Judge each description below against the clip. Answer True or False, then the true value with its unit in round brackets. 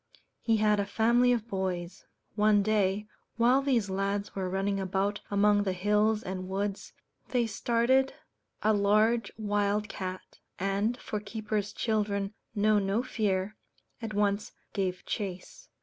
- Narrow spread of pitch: True (1.8 semitones)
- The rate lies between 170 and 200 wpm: False (135 wpm)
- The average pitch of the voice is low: False (205 Hz)